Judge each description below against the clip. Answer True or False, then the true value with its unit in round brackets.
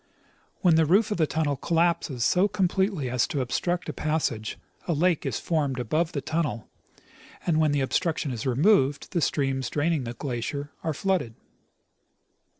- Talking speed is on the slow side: False (160 wpm)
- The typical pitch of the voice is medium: True (155 Hz)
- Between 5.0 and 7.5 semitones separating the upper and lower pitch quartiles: False (4.3 semitones)